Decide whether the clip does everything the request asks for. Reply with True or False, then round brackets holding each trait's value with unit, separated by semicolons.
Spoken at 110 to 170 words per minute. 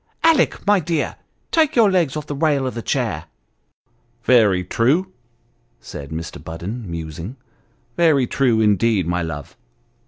True (155 wpm)